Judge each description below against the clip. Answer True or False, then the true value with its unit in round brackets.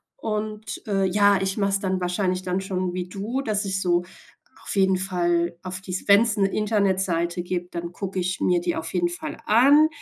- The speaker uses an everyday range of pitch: False (2.3 semitones)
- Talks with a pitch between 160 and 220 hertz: True (190 Hz)